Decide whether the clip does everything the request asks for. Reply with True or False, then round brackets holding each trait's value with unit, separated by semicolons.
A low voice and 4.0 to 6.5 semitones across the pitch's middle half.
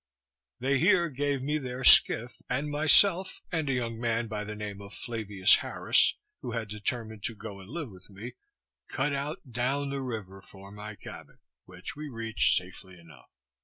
True (115 Hz; 5.0 semitones)